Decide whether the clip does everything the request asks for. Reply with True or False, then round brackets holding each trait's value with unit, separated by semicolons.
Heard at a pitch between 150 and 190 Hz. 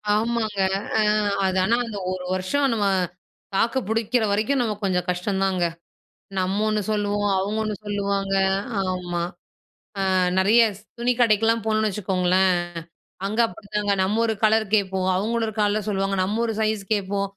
False (205 Hz)